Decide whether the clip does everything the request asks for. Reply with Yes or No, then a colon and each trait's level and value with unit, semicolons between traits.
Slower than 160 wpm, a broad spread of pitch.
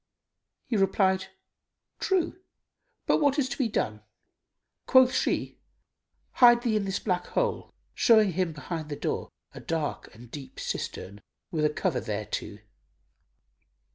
Yes: slow, 135 wpm; wide, 8.0 semitones